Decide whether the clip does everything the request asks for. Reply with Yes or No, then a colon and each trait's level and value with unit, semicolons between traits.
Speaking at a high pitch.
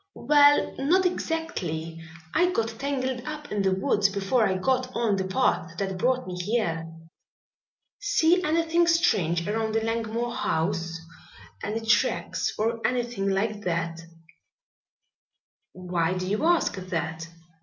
Yes: high, 220 Hz